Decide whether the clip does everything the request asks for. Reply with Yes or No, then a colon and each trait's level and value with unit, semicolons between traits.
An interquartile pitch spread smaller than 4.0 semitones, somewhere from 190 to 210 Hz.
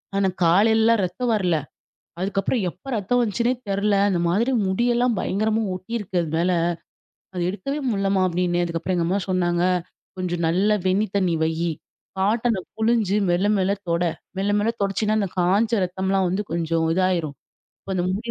Yes: average, 3.5 semitones; high, 195 Hz